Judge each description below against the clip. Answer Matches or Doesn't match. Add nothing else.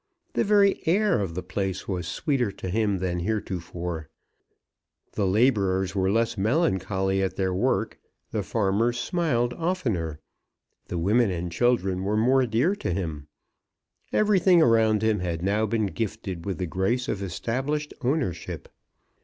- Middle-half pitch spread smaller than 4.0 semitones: Doesn't match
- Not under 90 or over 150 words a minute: Matches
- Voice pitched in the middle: Doesn't match